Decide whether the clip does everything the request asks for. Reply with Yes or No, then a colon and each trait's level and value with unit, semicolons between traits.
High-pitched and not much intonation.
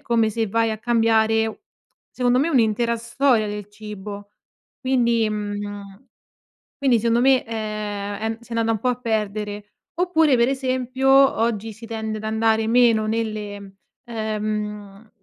Yes: high, 225 Hz; narrow, 2.2 semitones